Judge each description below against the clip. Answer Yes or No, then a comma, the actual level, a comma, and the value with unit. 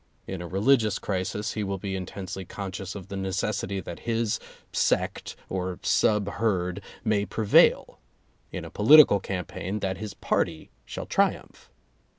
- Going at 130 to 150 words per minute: Yes, average, 145 wpm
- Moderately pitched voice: No, low, 100 Hz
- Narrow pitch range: Yes, narrow, 2.2 semitones